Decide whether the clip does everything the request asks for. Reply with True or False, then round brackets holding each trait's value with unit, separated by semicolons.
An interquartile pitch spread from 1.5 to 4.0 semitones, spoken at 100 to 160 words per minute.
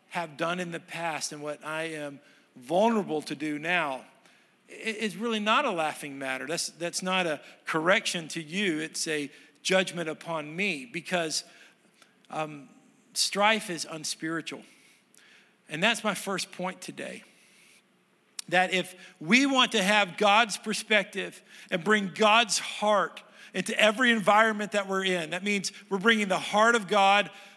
False (4.5 semitones; 150 wpm)